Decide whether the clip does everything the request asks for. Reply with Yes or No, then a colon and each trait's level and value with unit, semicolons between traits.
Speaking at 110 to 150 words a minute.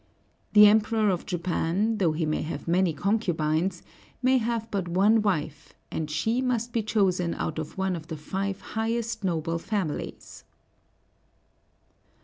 Yes: average, 140 wpm